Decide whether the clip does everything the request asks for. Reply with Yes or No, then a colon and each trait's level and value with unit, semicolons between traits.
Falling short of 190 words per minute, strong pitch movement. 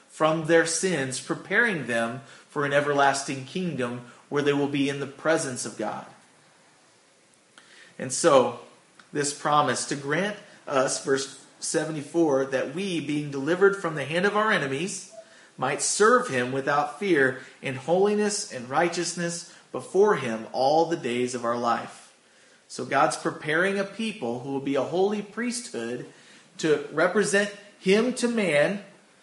Yes: average, 145 wpm; wide, 5.9 semitones